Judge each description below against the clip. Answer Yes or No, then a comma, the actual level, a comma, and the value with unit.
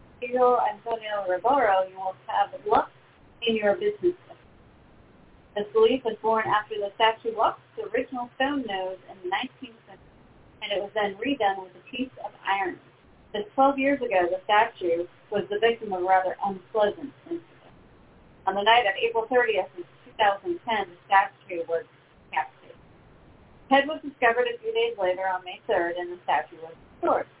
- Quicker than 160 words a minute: Yes, average, 170 wpm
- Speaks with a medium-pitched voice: No, high, 215 Hz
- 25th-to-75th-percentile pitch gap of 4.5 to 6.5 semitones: Yes, average, 4.8 semitones